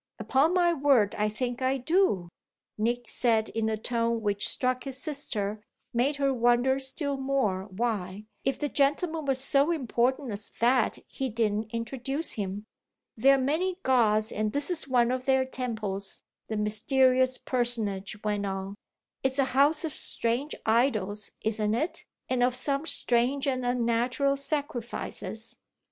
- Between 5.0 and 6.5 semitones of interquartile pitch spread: No, average, 3.9 semitones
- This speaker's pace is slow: No, average, 155 wpm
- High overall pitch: Yes, high, 245 Hz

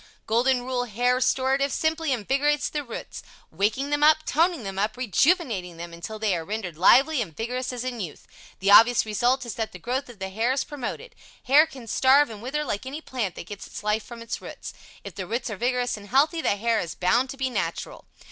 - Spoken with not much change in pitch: No, average, 4.5 semitones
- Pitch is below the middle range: No, high, 245 Hz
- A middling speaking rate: No, fast, 220 wpm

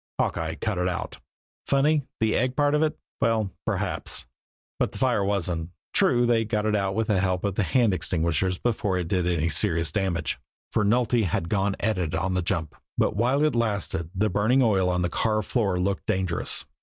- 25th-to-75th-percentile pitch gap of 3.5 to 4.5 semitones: Yes, average, 4.0 semitones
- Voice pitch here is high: No, low, 100 Hz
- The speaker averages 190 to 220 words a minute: Yes, average, 200 wpm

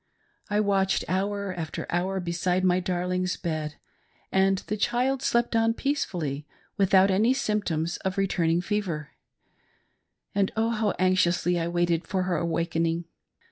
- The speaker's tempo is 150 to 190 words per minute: No, average, 140 wpm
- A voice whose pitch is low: No, medium, 185 Hz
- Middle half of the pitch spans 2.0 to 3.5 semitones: Yes, average, 2.9 semitones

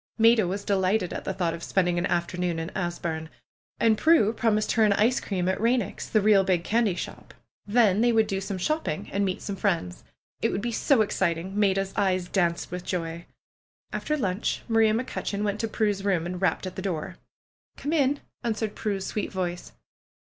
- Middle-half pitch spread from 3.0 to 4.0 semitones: Yes, average, 3.5 semitones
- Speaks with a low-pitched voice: No, high, 195 Hz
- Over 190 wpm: Yes, average, 200 wpm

